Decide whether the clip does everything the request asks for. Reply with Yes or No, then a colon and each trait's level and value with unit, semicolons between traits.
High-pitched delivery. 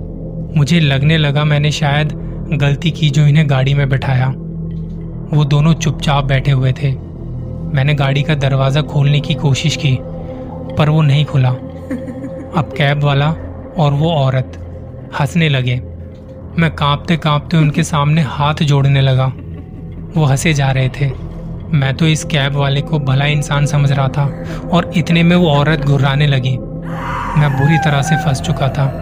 No: medium, 145 Hz